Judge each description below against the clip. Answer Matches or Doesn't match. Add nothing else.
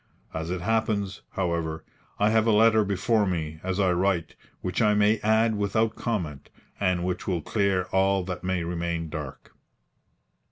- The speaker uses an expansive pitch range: Doesn't match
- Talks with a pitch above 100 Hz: Doesn't match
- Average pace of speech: Matches